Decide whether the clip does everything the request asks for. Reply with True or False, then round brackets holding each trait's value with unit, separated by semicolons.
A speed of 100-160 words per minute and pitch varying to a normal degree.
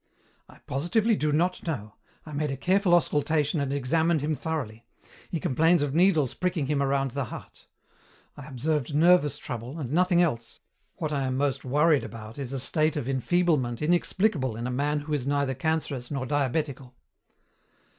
False (170 wpm; 3.5 semitones)